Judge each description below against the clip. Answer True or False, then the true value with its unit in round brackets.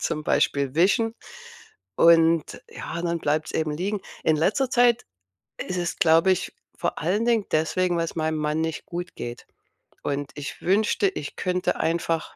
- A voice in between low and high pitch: True (170 Hz)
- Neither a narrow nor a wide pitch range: True (3.1 semitones)